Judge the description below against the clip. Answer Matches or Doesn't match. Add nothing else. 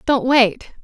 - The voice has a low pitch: Doesn't match